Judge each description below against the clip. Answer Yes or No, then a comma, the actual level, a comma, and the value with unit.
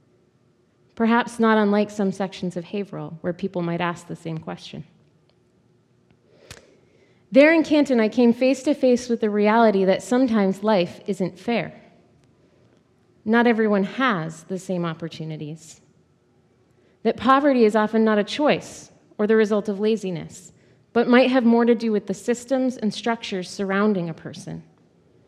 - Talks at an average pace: Yes, average, 145 wpm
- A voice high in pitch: Yes, high, 210 Hz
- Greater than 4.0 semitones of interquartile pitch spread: Yes, average, 4.4 semitones